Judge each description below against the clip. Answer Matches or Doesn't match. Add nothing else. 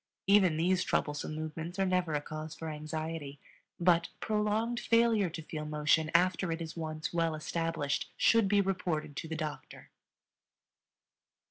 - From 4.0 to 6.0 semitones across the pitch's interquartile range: Doesn't match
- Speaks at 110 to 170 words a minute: Matches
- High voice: Doesn't match